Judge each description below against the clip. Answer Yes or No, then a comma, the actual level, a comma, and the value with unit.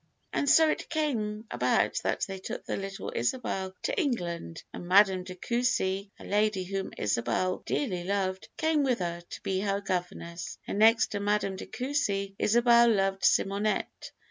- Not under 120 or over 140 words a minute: No, average, 165 wpm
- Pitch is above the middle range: Yes, high, 200 Hz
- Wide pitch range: No, average, 4.0 semitones